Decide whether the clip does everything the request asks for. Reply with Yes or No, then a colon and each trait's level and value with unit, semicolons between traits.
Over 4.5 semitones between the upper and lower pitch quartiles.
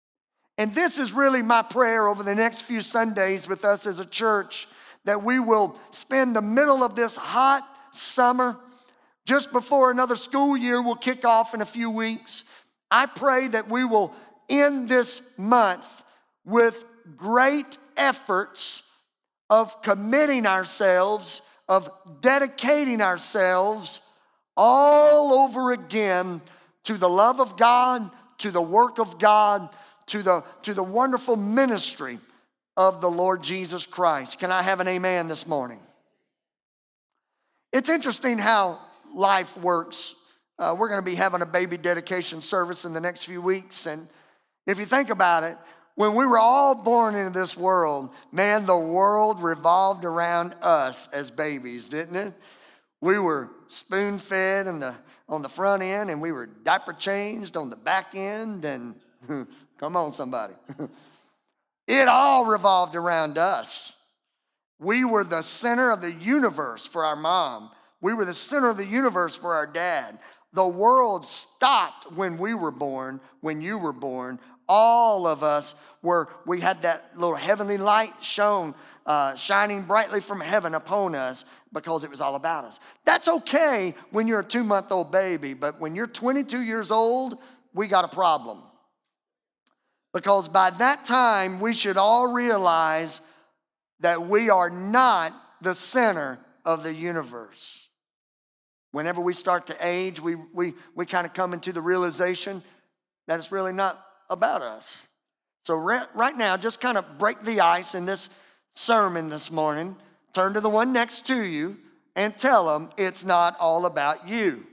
Yes: average, 5.1 semitones